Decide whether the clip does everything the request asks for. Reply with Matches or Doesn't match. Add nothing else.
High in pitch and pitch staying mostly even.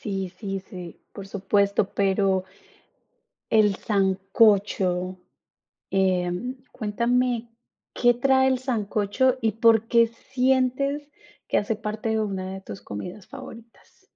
Doesn't match